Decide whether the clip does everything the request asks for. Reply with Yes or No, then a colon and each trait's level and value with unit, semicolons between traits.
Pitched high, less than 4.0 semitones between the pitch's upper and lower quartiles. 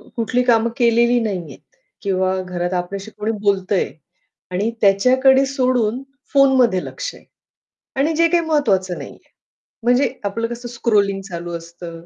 No: high, 225 Hz; average, 5.1 semitones